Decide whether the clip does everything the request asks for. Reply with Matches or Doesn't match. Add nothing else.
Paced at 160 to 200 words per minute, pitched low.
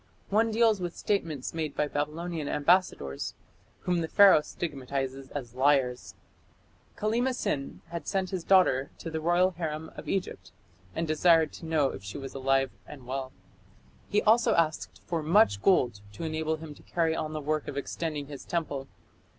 Doesn't match